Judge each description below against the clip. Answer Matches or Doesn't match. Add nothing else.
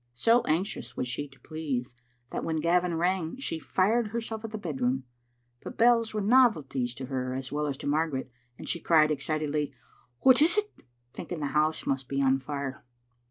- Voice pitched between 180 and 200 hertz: Doesn't match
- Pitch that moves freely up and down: Matches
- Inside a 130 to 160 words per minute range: Doesn't match